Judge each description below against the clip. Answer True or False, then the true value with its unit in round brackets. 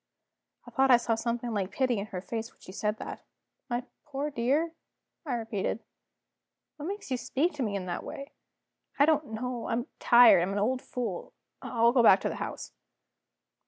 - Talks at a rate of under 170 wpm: False (190 wpm)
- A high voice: True (240 Hz)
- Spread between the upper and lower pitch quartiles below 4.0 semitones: True (3.3 semitones)